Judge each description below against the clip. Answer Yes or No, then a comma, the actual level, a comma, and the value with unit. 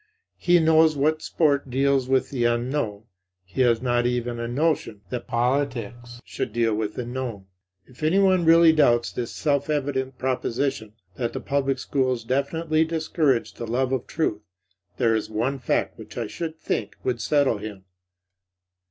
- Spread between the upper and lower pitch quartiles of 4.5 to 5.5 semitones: No, average, 3.6 semitones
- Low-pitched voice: Yes, low, 130 Hz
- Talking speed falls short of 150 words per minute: No, average, 160 wpm